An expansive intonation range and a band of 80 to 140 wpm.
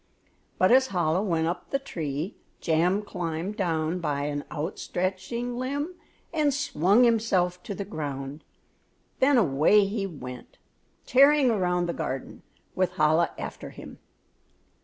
Yes: wide, 6.4 semitones; slow, 135 wpm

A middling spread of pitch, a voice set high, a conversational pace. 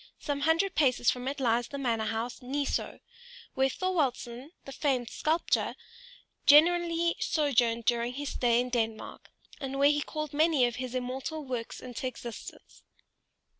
Yes: average, 3.6 semitones; very high, 265 Hz; average, 150 wpm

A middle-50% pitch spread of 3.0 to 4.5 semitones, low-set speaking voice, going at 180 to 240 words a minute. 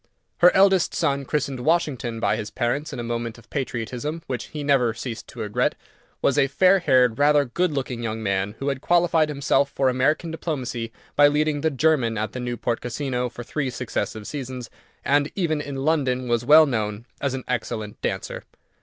Yes: average, 3.9 semitones; low, 130 Hz; average, 185 wpm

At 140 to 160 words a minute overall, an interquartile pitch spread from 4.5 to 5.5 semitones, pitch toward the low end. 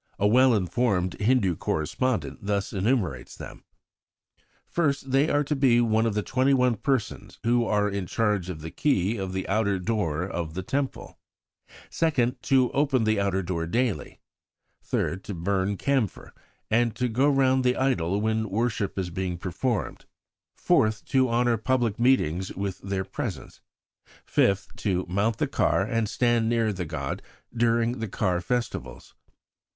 Yes: average, 150 wpm; average, 4.8 semitones; low, 110 Hz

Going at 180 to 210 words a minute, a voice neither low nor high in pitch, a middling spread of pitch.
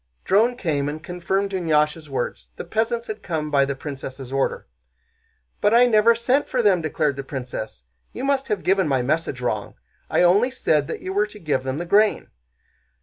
No: average, 190 wpm; medium, 170 Hz; wide, 7.1 semitones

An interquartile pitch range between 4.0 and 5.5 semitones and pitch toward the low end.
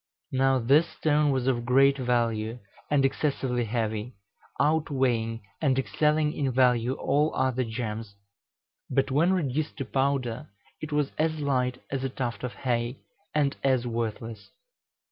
No: average, 3.1 semitones; low, 130 Hz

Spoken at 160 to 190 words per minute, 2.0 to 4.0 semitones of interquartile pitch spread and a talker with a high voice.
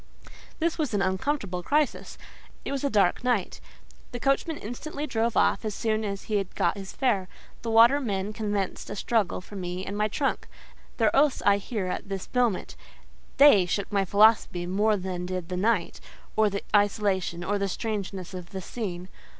Yes: average, 180 wpm; average, 3.6 semitones; high, 205 Hz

